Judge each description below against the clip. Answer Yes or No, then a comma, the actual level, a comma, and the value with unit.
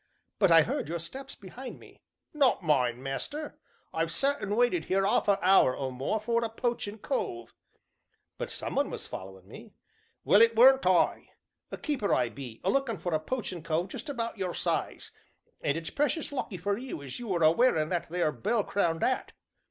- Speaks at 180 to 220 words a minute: Yes, average, 200 wpm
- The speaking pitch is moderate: No, high, 195 Hz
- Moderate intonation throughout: No, wide, 7.4 semitones